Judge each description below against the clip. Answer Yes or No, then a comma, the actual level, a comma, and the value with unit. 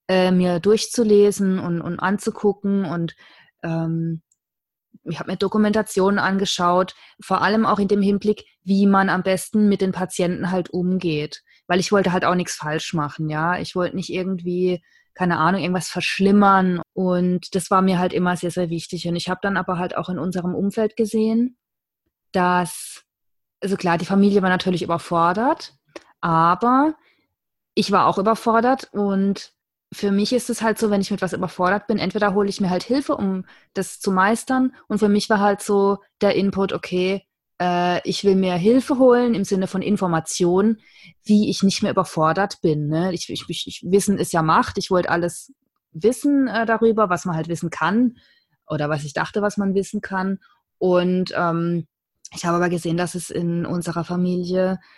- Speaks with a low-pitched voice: No, medium, 185 Hz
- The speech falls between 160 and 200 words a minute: Yes, average, 180 wpm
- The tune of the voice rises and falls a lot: No, average, 2.7 semitones